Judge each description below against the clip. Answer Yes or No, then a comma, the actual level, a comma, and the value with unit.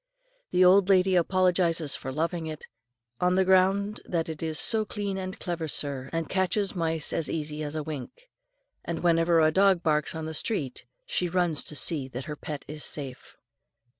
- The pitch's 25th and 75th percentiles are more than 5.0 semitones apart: No, average, 3.3 semitones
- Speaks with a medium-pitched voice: Yes, medium, 165 Hz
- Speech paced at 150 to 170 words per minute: No, average, 180 wpm